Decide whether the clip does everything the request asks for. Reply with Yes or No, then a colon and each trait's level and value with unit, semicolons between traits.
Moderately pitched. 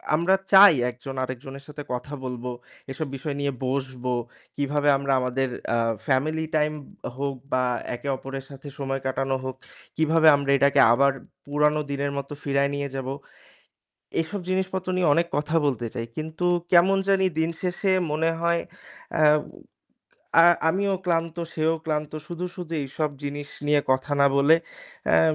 Yes: medium, 145 Hz